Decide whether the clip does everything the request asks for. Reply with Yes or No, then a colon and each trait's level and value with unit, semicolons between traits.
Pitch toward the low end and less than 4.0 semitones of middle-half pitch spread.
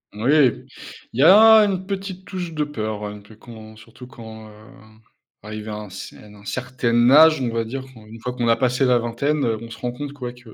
No: low, 120 Hz; average, 4.6 semitones